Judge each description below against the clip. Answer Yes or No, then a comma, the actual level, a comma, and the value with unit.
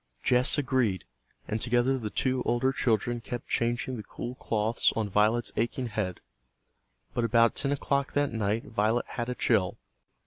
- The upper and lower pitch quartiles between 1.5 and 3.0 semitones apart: Yes, narrow, 2.6 semitones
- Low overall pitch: Yes, low, 120 Hz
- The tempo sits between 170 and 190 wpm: No, average, 160 wpm